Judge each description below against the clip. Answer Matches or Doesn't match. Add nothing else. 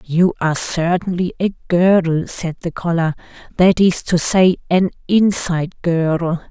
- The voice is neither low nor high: Matches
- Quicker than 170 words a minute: Doesn't match